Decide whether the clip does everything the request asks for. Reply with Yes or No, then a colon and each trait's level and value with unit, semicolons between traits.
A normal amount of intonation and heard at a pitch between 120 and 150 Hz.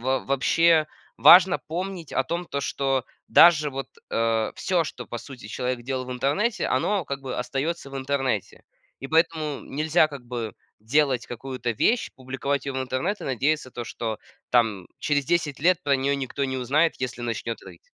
Yes: average, 3.7 semitones; low, 135 Hz